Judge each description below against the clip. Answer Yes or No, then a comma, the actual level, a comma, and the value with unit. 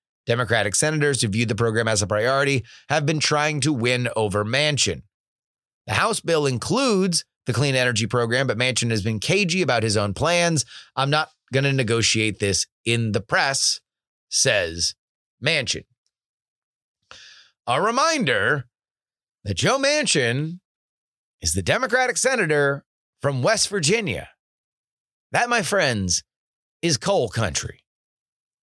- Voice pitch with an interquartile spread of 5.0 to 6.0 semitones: Yes, wide, 5.5 semitones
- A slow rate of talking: Yes, slow, 130 wpm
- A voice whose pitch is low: Yes, low, 130 Hz